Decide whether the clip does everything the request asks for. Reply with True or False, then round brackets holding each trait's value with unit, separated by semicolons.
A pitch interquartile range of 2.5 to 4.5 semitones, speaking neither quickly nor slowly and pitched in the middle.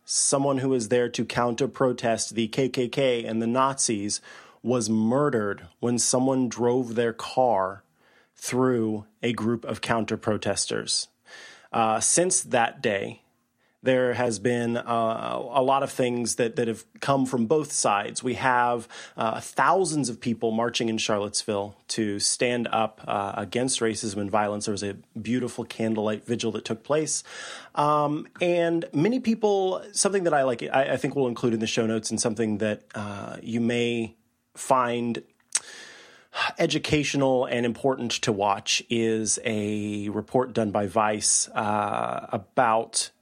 False (2.8 semitones; 150 wpm; 120 Hz)